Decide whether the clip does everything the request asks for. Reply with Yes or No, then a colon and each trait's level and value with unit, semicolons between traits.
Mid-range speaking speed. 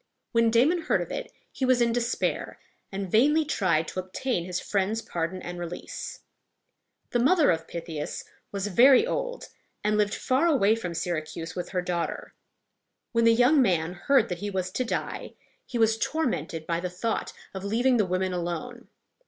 Yes: average, 175 wpm